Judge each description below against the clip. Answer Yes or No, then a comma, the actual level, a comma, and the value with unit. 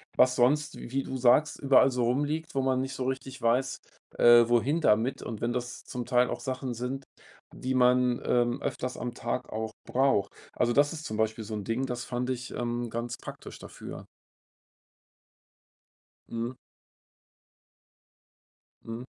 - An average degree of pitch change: No, narrow, 1.9 semitones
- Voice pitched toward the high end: No, low, 125 Hz